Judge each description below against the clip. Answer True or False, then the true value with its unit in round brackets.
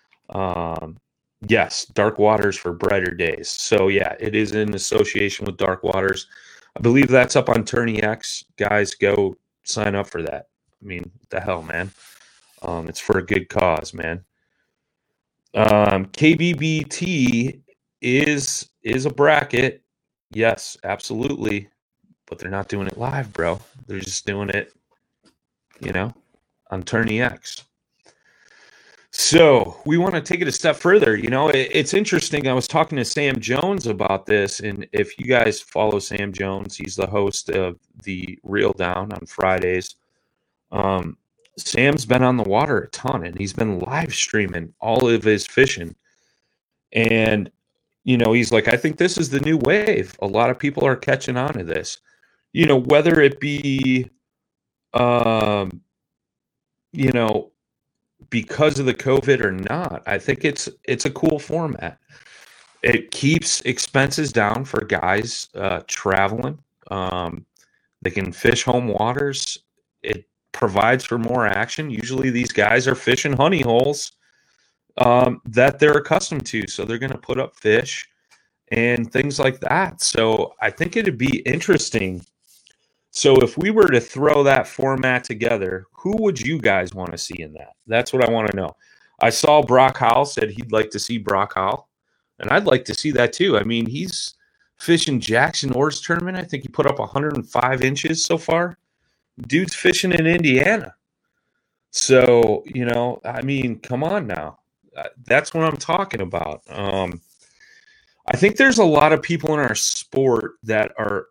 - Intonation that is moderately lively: False (6.2 semitones)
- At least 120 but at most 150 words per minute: False (160 wpm)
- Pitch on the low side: True (120 Hz)